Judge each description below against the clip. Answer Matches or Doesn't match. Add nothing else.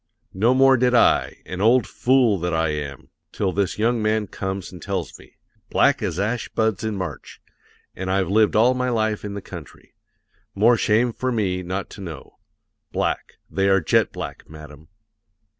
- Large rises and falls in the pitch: Doesn't match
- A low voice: Matches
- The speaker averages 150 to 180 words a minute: Matches